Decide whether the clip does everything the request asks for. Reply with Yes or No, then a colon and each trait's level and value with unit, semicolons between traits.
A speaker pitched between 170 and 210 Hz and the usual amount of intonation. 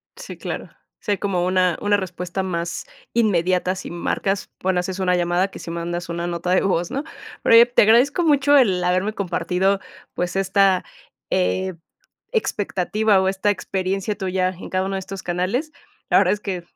No: high, 190 Hz; narrow, 2.2 semitones